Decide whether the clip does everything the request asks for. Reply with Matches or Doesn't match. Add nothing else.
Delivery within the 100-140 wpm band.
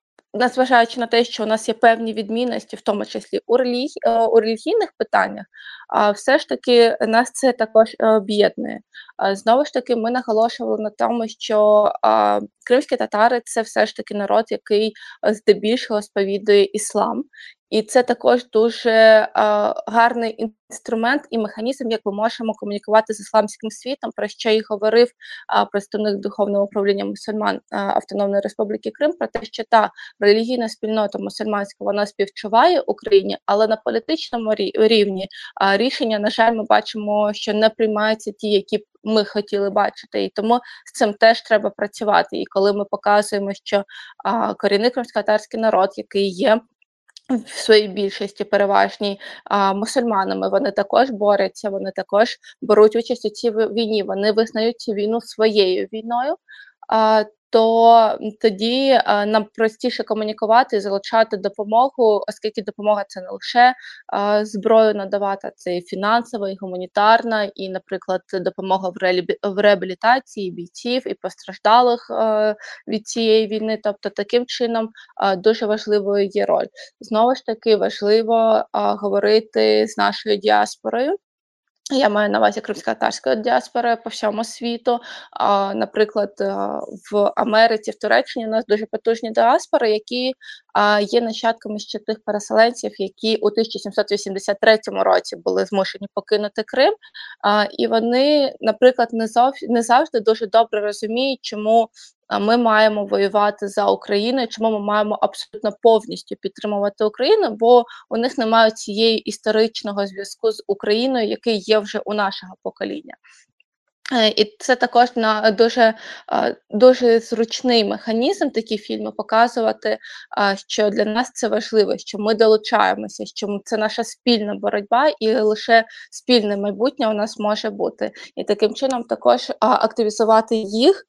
Matches